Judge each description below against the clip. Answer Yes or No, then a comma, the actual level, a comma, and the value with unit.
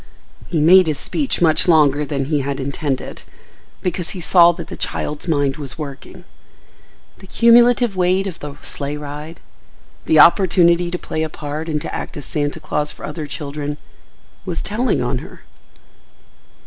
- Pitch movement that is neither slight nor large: Yes, average, 3.4 semitones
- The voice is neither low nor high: Yes, medium, 155 Hz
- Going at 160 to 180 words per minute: Yes, average, 165 wpm